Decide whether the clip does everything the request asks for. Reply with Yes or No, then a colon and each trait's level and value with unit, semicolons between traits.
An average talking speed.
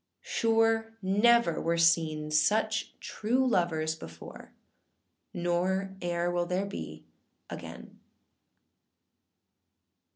No: slow, 85 wpm